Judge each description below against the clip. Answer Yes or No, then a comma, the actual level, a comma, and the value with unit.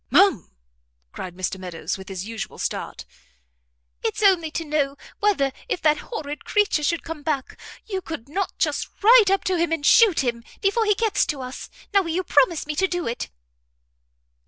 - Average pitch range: No, wide, 6.5 semitones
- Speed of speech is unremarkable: Yes, average, 180 wpm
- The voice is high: Yes, very high, 320 Hz